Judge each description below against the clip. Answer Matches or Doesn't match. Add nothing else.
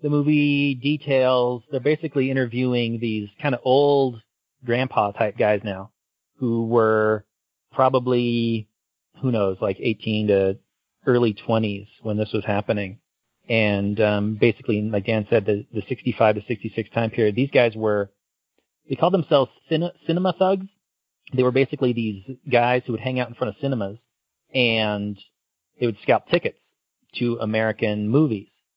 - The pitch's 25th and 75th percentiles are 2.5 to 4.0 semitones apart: Matches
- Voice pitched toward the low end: Matches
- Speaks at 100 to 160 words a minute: Matches